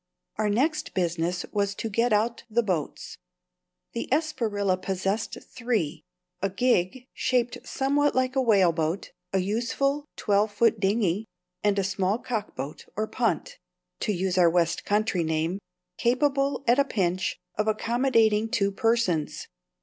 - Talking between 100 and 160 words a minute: Yes, slow, 135 wpm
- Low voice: No, high, 210 Hz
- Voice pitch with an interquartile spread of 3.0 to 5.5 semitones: Yes, average, 4.4 semitones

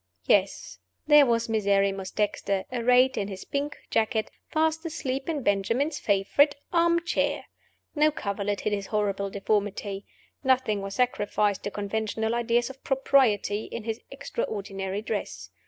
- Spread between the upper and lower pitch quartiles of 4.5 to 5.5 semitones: Yes, average, 4.9 semitones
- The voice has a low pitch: No, high, 220 Hz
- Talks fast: No, slow, 135 wpm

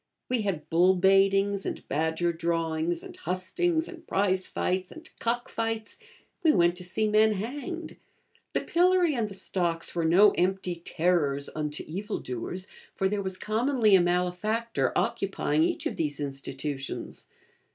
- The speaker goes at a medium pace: Yes, average, 150 wpm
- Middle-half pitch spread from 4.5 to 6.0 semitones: Yes, average, 4.8 semitones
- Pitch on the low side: No, high, 190 Hz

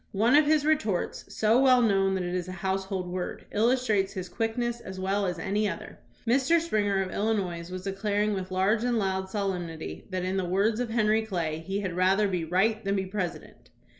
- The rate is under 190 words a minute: No, fast, 205 wpm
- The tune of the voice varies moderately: Yes, average, 3.0 semitones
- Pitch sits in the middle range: No, high, 195 Hz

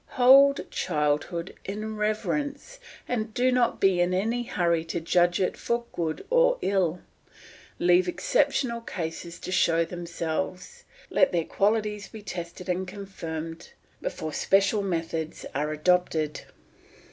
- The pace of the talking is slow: Yes, slow, 125 wpm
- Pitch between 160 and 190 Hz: Yes, medium, 185 Hz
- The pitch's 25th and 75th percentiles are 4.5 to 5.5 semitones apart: Yes, average, 4.9 semitones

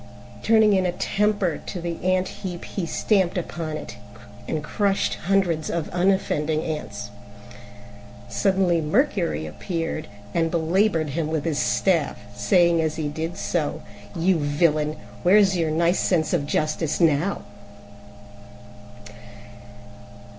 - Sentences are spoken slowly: Yes, slow, 120 wpm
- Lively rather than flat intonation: No, average, 3.3 semitones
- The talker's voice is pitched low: No, medium, 170 Hz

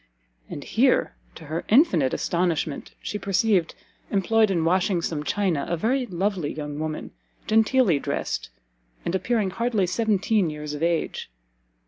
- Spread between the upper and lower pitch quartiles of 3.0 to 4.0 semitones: No, average, 5.1 semitones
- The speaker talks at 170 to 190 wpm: No, slow, 135 wpm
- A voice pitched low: No, medium, 185 Hz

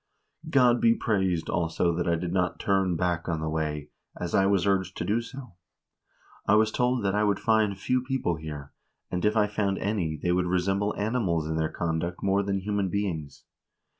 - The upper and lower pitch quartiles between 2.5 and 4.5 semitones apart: Yes, average, 3.5 semitones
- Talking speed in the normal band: Yes, average, 195 wpm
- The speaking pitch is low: Yes, very low, 95 Hz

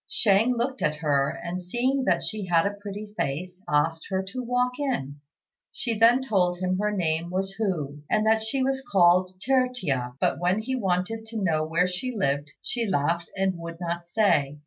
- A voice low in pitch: No, high, 190 Hz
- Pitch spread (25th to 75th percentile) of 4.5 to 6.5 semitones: Yes, average, 5.1 semitones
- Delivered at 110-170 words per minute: No, average, 190 wpm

